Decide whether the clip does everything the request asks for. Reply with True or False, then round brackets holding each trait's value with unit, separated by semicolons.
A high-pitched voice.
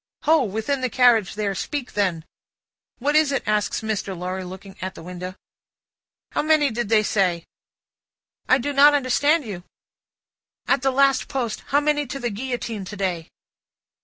True (230 Hz)